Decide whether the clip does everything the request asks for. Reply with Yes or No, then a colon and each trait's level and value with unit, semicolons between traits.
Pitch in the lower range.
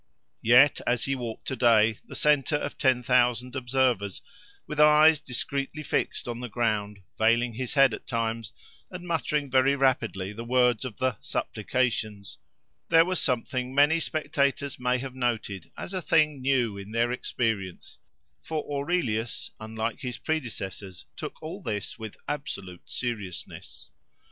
Yes: low, 125 Hz